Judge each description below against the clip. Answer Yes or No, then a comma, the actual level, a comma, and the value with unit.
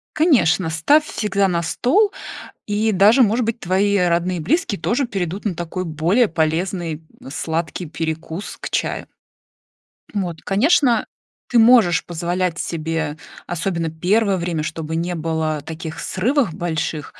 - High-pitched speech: No, medium, 175 Hz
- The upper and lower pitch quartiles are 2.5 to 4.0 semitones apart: No, average, 4.6 semitones